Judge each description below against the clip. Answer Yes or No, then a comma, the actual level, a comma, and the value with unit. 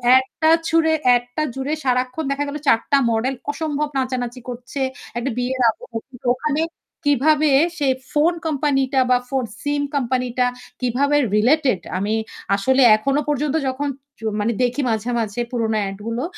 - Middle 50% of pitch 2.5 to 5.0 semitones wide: Yes, average, 2.9 semitones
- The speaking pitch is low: No, very high, 260 Hz